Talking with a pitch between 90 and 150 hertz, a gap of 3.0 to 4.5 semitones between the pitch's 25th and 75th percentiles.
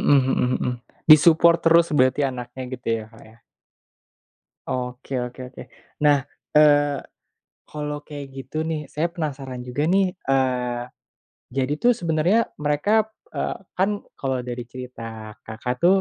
Yes: low, 135 Hz; average, 3.6 semitones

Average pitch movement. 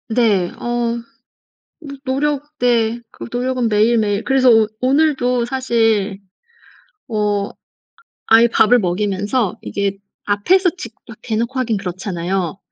Yes: average, 3.9 semitones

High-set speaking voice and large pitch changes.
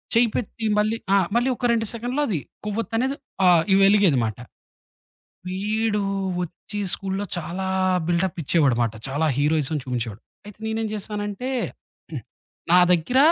Yes: high, 195 Hz; wide, 5.7 semitones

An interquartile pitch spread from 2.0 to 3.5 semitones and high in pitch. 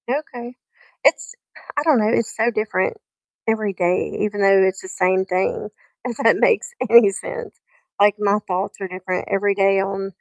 Yes: average, 3.2 semitones; high, 200 Hz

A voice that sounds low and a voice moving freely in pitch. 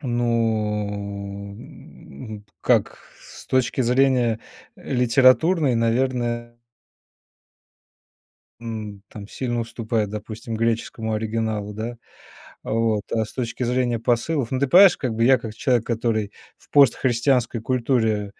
No: low, 115 Hz; narrow, 2.5 semitones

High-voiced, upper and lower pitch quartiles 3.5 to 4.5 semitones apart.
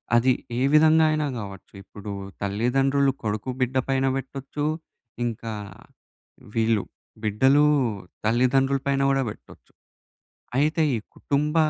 No: low, 135 Hz; average, 3.8 semitones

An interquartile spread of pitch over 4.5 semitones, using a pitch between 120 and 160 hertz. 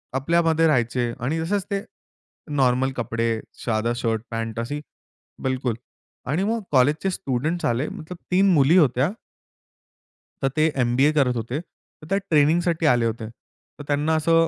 Yes: average, 5.2 semitones; medium, 140 Hz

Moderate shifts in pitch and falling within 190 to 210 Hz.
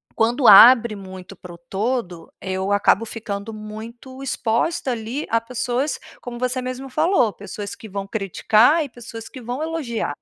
No: average, 3.9 semitones; high, 230 Hz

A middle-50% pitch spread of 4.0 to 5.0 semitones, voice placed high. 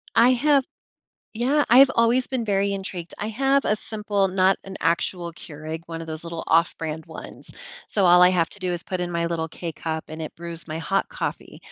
No: average, 4.5 semitones; medium, 180 Hz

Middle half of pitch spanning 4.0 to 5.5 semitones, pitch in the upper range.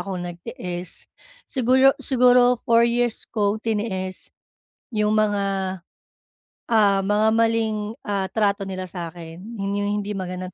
No: average, 3.4 semitones; high, 205 Hz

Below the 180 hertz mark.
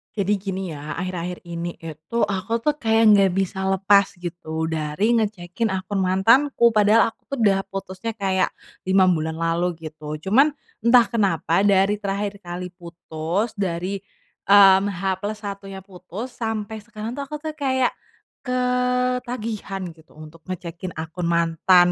No: high, 195 Hz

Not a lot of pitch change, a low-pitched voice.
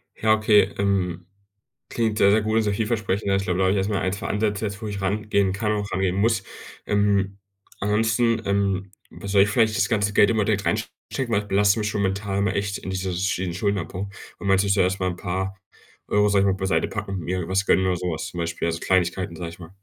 Yes: narrow, 1.8 semitones; low, 100 Hz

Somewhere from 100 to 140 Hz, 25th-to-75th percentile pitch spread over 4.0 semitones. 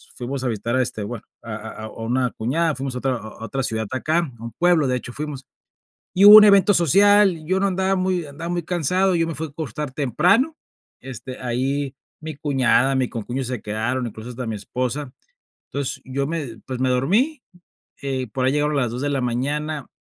Yes: low, 135 Hz; average, 4.9 semitones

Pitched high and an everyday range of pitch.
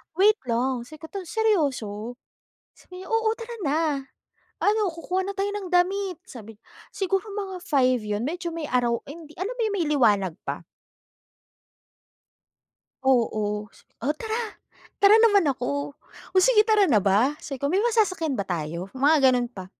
No: very high, 315 Hz; wide, 8.6 semitones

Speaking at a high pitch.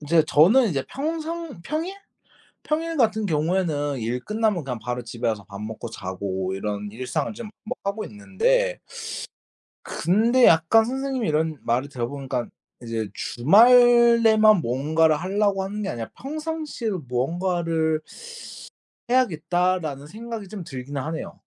No: medium, 175 Hz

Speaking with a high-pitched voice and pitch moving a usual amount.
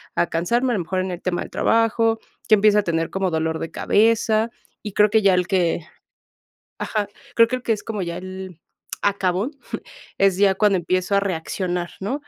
Yes: high, 195 Hz; average, 3.3 semitones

